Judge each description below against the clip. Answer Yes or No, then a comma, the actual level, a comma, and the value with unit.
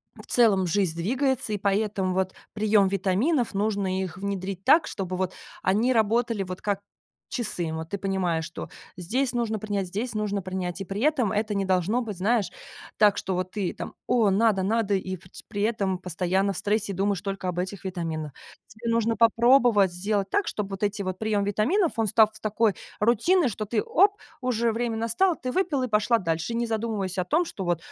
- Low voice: No, high, 205 Hz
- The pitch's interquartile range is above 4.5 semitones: No, average, 3.4 semitones